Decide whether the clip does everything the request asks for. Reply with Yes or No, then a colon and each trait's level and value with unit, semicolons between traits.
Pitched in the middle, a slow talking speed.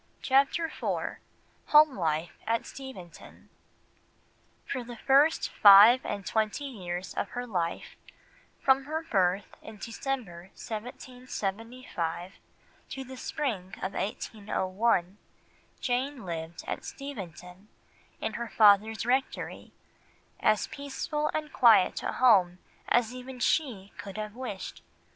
No: high, 225 Hz; slow, 110 wpm